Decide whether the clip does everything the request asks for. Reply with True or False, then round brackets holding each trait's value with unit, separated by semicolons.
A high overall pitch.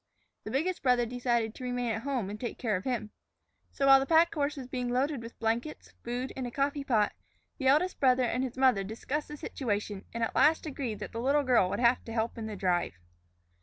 True (250 Hz)